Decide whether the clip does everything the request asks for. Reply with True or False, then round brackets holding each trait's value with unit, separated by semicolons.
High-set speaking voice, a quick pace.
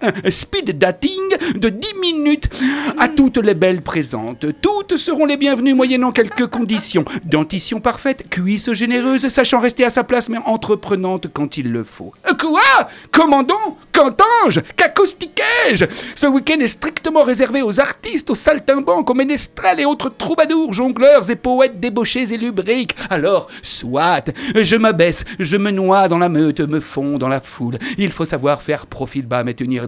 False (245 Hz; 160 wpm)